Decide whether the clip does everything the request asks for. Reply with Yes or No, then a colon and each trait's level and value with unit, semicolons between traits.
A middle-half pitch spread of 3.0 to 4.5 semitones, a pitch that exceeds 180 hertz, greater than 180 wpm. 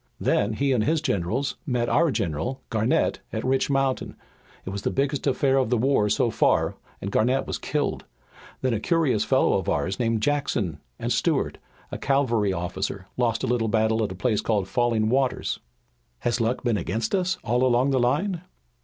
No: average, 3.9 semitones; low, 120 Hz; average, 190 wpm